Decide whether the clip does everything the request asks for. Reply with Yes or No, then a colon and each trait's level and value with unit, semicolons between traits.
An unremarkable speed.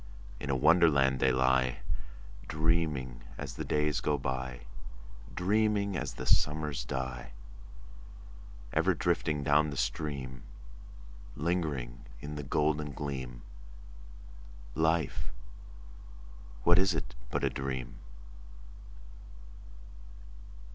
No: slow, 95 wpm